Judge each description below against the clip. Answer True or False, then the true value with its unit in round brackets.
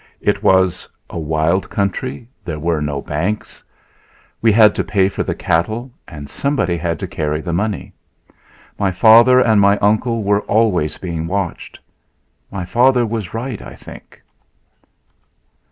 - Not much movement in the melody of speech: False (4.9 semitones)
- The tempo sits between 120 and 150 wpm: True (145 wpm)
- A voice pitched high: False (100 Hz)